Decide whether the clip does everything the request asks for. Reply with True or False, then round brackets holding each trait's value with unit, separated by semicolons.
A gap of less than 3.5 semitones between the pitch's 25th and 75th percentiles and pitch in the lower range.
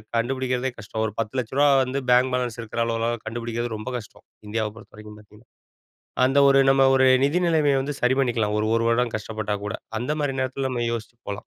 True (3.1 semitones; 120 Hz)